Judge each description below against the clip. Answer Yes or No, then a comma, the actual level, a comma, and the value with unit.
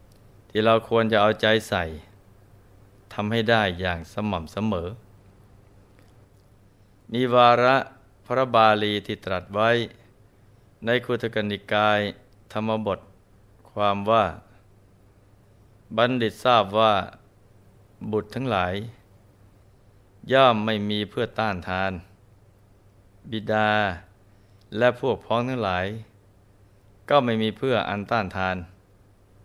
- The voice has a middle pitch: No, low, 105 Hz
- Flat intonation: Yes, narrow, 1.9 semitones